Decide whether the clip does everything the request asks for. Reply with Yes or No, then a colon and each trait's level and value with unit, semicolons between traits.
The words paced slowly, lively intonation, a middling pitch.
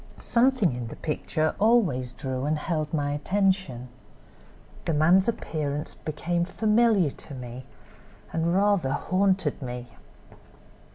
Yes: slow, 115 wpm; wide, 5.8 semitones; medium, 155 Hz